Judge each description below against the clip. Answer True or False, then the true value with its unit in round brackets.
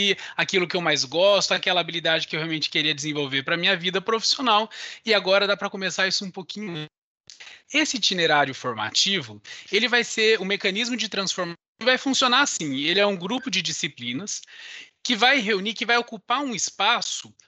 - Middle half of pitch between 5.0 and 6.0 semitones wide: True (5.3 semitones)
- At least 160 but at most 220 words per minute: True (180 wpm)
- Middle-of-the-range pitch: False (195 Hz)